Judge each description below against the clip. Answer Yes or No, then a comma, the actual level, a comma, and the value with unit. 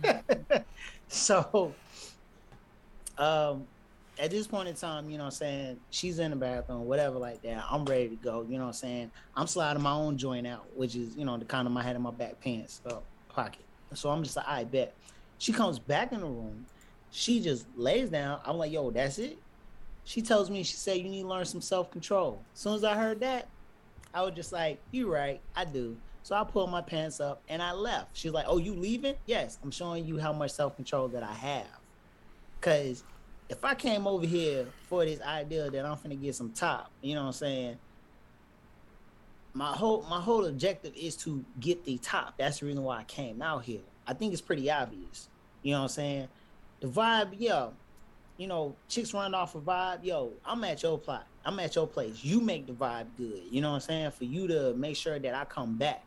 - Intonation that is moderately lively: No, wide, 5.9 semitones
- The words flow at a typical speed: No, fast, 225 wpm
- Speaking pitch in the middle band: Yes, medium, 150 Hz